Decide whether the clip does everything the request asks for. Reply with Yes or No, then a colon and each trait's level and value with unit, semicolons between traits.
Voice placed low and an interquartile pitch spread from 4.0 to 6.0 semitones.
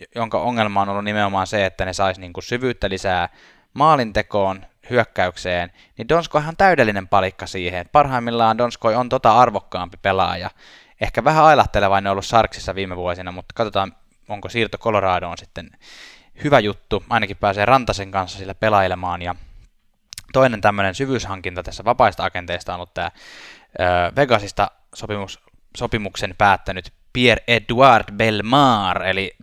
No: low, 105 Hz; average, 3.6 semitones